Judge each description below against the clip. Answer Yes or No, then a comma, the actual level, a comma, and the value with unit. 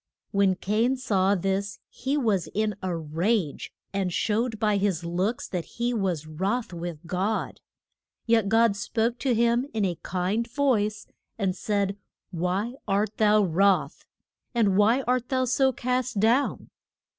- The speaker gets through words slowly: No, average, 145 wpm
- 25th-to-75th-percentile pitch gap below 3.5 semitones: No, average, 3.8 semitones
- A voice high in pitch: Yes, high, 210 Hz